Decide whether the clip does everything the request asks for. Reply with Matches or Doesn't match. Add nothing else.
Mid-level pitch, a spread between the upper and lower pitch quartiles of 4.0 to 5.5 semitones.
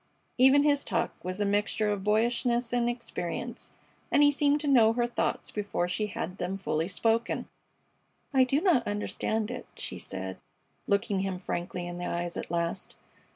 Doesn't match